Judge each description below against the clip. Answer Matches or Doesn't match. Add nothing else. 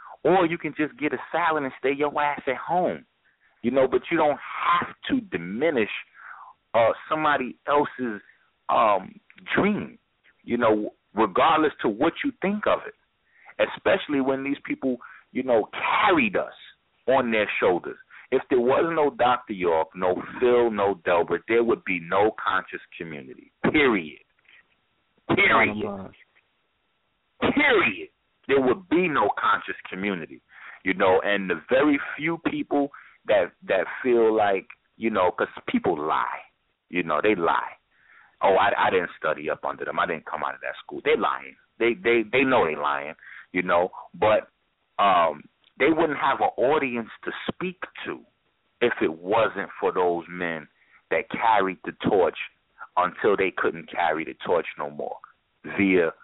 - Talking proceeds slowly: Doesn't match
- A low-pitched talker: Matches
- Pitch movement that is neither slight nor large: Doesn't match